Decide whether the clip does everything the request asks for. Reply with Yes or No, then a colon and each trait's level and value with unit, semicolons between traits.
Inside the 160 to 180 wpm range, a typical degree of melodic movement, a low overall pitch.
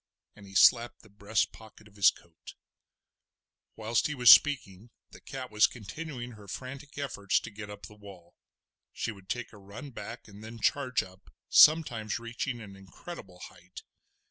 Yes: average, 170 wpm; average, 3.6 semitones; low, 110 Hz